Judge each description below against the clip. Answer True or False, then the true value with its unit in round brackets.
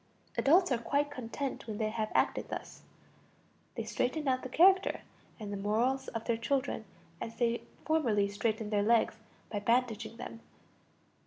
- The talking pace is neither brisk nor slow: True (155 wpm)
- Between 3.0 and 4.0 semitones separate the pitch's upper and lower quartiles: True (3.6 semitones)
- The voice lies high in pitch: True (235 Hz)